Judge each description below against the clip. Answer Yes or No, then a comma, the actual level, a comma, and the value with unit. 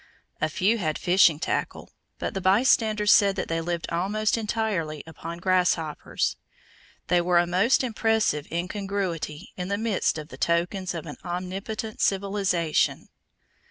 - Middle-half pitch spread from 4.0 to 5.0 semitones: No, average, 3.5 semitones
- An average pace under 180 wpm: Yes, average, 140 wpm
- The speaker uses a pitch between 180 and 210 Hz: Yes, medium, 185 Hz